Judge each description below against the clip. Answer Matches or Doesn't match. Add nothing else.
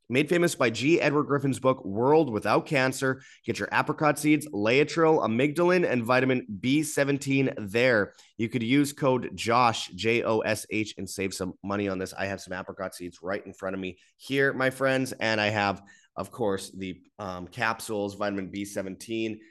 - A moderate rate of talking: Matches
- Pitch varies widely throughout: Matches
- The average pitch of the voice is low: Matches